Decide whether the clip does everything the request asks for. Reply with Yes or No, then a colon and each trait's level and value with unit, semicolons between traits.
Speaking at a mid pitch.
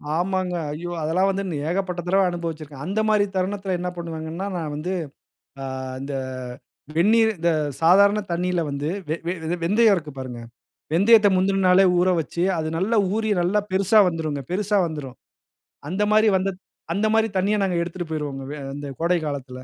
Yes: medium, 180 Hz